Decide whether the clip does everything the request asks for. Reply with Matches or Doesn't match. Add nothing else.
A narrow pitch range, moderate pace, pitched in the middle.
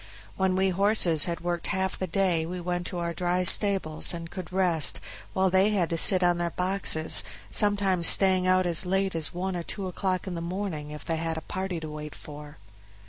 Doesn't match